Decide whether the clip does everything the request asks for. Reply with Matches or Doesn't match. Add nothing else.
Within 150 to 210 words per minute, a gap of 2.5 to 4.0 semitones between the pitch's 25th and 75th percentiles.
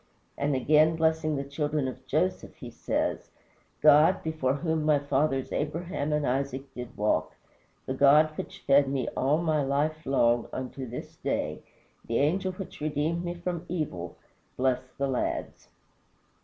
Matches